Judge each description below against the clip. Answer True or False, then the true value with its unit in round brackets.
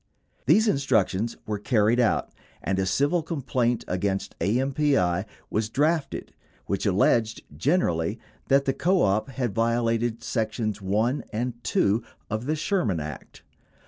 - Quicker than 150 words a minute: False (135 wpm)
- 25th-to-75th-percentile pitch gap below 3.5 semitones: False (5.3 semitones)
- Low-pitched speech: True (115 Hz)